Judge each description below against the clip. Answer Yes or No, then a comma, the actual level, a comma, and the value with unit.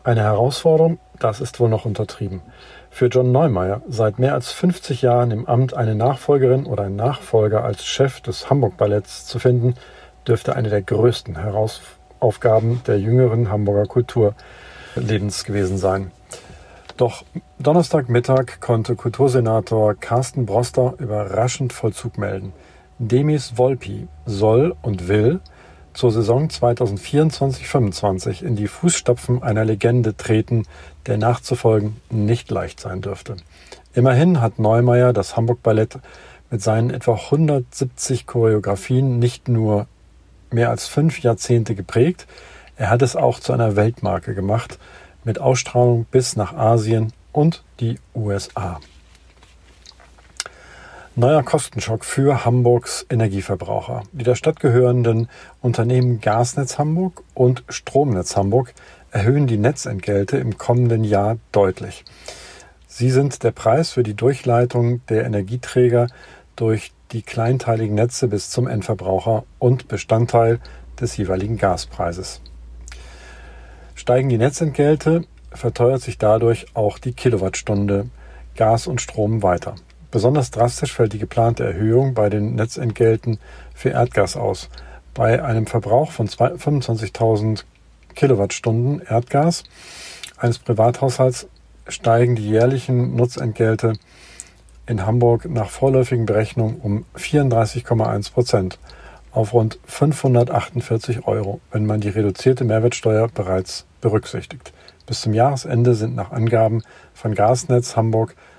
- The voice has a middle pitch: No, low, 115 Hz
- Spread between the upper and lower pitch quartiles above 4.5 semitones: No, average, 3.1 semitones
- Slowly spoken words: Yes, slow, 115 wpm